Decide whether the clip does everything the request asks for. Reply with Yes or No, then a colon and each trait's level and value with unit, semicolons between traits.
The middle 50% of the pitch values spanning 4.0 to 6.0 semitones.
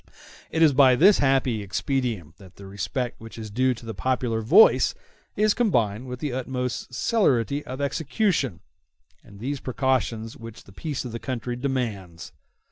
No: average, 3.4 semitones